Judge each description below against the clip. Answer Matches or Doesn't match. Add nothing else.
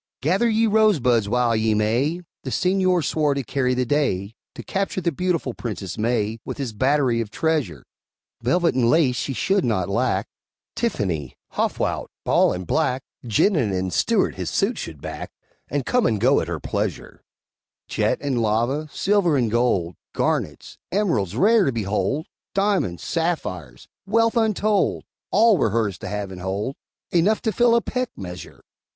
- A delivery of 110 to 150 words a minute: Doesn't match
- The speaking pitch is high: Doesn't match